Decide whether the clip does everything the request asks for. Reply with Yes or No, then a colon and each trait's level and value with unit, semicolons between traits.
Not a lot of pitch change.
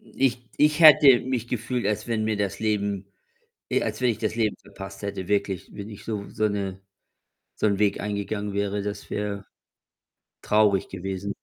Yes: narrow, 1.9 semitones